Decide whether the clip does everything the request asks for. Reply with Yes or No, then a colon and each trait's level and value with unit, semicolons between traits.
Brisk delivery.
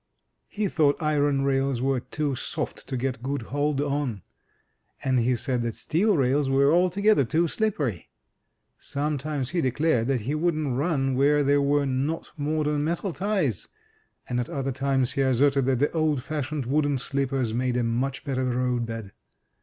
No: average, 165 wpm